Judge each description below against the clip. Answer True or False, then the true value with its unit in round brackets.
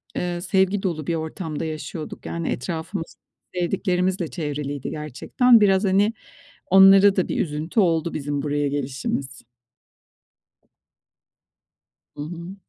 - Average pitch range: True (4.1 semitones)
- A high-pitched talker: False (170 Hz)